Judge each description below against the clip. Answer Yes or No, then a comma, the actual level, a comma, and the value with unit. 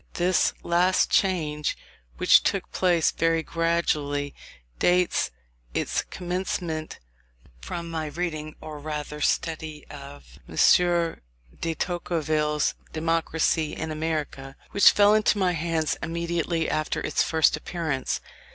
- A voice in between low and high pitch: Yes, medium, 160 Hz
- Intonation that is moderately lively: No, narrow, 2.2 semitones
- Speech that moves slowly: Yes, slow, 110 wpm